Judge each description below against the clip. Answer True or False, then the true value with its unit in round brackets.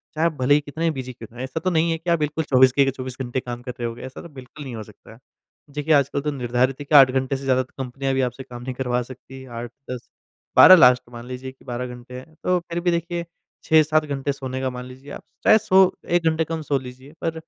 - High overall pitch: False (135 Hz)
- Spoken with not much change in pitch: False (3.6 semitones)